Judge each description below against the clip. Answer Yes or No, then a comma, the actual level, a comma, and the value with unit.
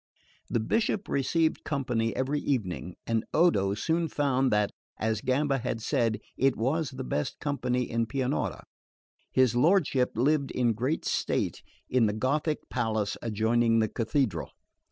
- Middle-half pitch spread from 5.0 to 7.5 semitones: No, average, 4.0 semitones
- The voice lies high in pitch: No, low, 125 Hz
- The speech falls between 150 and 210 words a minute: No, average, 140 wpm